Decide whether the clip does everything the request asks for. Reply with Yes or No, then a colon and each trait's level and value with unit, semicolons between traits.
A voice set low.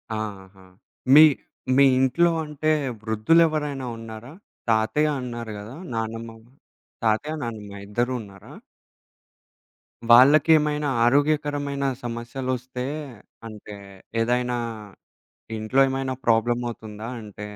Yes: low, 120 Hz